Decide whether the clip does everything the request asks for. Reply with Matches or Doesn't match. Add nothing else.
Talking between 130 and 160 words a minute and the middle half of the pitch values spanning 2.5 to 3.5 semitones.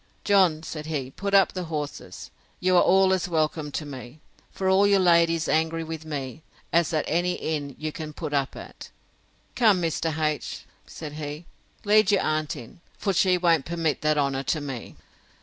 Doesn't match